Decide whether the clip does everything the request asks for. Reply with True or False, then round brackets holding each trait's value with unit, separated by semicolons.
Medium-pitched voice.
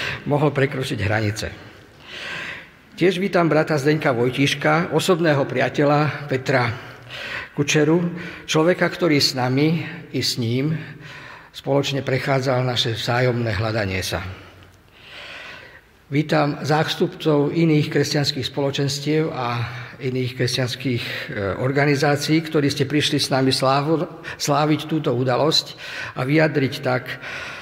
True (145 Hz)